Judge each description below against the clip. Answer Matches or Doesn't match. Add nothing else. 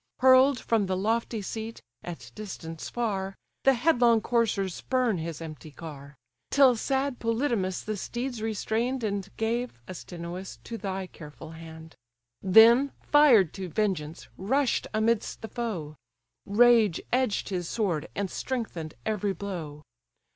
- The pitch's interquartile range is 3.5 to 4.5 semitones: Doesn't match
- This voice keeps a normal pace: Doesn't match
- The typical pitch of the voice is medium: Doesn't match